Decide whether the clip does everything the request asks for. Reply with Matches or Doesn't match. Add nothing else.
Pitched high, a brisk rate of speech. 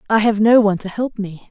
Matches